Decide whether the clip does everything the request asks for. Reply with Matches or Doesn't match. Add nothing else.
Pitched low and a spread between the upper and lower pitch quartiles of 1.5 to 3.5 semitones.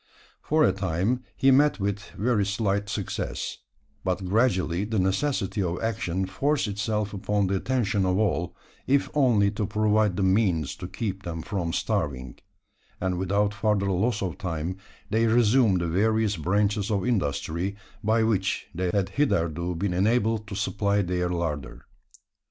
Matches